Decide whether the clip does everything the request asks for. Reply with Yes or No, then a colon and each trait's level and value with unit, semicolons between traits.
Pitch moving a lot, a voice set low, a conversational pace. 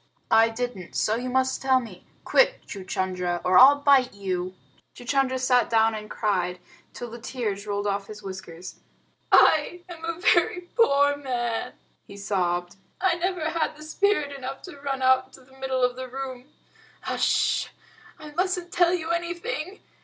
No: wide, 6.6 semitones; very high, 255 Hz; average, 160 wpm